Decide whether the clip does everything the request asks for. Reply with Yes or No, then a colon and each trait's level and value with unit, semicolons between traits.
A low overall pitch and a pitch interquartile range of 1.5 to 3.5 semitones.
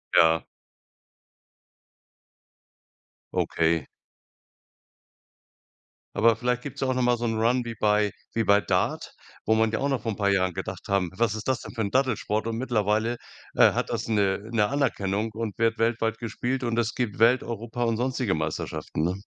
Yes: low, 115 Hz; average, 2.8 semitones